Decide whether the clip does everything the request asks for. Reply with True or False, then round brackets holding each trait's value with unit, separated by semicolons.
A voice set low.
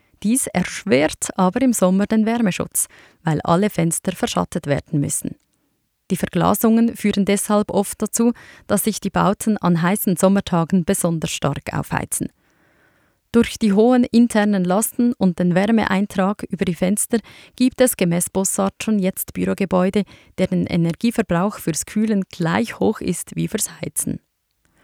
False (195 Hz)